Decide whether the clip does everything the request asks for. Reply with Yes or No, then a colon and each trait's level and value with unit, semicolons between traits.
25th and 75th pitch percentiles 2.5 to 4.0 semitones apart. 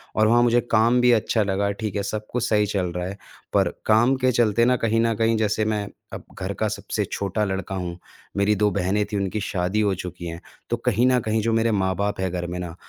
Yes: average, 2.8 semitones